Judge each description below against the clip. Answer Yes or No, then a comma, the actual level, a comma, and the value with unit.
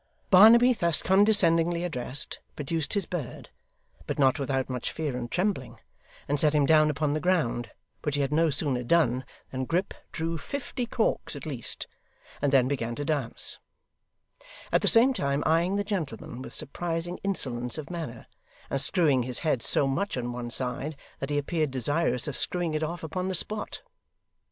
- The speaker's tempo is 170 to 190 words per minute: Yes, average, 175 wpm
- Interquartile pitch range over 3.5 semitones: Yes, average, 4.7 semitones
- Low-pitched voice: No, medium, 155 Hz